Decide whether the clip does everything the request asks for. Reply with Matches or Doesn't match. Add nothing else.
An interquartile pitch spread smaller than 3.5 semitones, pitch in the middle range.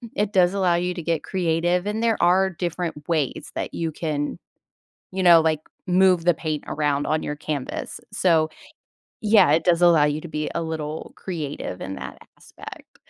Matches